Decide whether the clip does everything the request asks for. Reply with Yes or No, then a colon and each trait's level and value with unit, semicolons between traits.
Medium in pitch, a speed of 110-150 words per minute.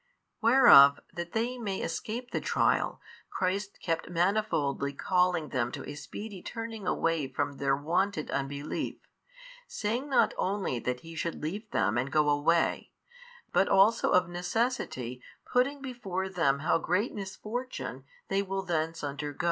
Yes: medium, 180 Hz; average, 140 wpm